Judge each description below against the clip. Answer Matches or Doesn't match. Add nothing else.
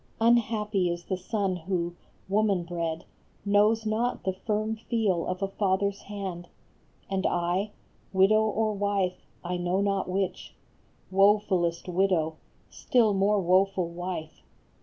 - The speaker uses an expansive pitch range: Doesn't match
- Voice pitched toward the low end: Doesn't match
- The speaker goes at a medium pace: Doesn't match